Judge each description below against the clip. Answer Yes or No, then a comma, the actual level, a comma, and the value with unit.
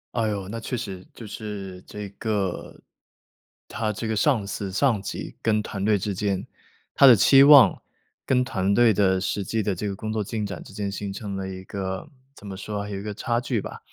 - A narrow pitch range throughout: Yes, narrow, 2.3 semitones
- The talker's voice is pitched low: Yes, low, 105 Hz